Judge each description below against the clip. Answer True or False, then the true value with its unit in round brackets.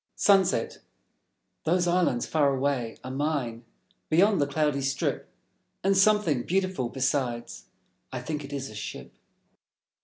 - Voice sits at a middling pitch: True (145 Hz)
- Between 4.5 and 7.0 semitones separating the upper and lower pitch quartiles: True (5.2 semitones)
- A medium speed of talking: False (125 wpm)